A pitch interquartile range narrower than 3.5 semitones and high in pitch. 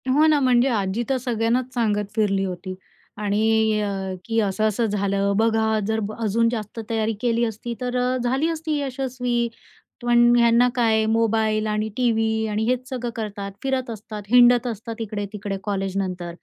Yes: narrow, 2.5 semitones; high, 225 Hz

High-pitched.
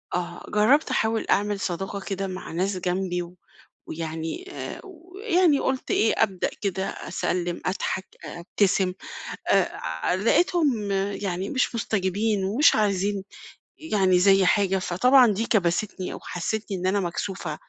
Yes: high, 195 Hz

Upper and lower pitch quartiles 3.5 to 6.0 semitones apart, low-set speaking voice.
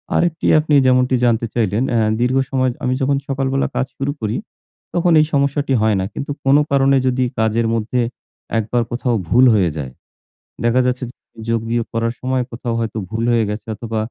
No: average, 2.9 semitones; low, 125 Hz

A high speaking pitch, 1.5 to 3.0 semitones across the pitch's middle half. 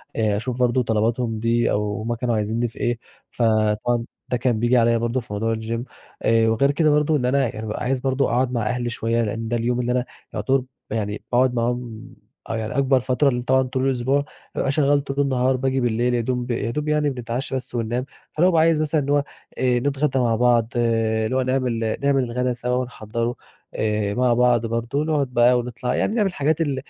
No: low, 125 Hz; narrow, 2.4 semitones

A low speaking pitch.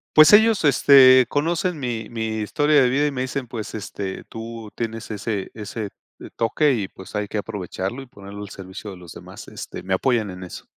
Yes: low, 115 Hz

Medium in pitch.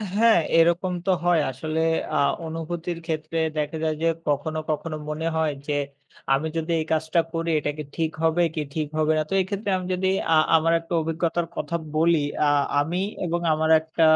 Yes: medium, 160 Hz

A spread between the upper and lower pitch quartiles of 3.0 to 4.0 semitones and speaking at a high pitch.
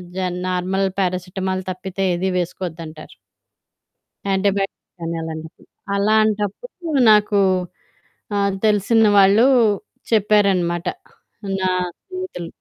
No: narrow, 2.6 semitones; high, 195 Hz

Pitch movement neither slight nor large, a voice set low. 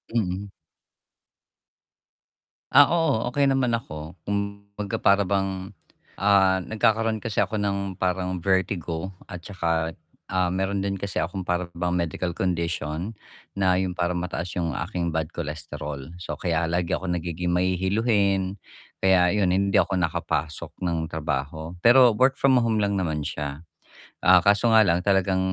Yes: average, 3.0 semitones; very low, 95 Hz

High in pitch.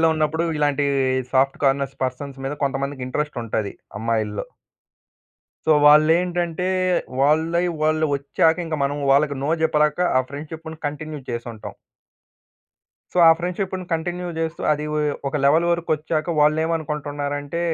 No: medium, 150 Hz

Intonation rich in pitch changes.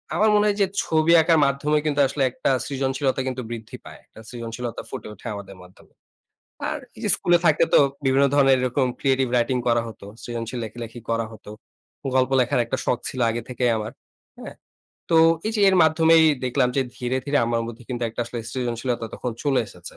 No: average, 3.4 semitones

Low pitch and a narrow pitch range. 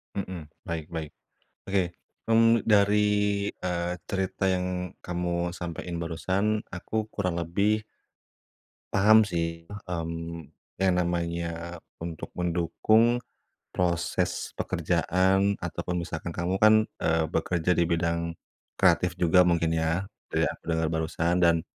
Yes: very low, 85 Hz; narrow, 2.3 semitones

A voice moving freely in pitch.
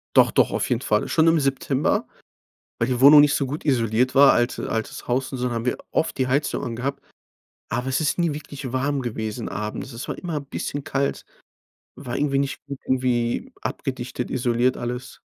No: average, 2.7 semitones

